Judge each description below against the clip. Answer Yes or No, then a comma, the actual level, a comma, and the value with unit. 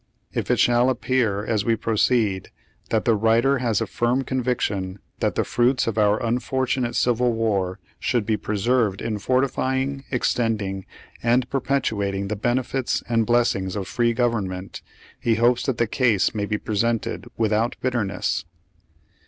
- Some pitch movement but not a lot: Yes, average, 3.0 semitones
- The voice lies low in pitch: Yes, low, 115 Hz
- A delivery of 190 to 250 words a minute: No, average, 150 wpm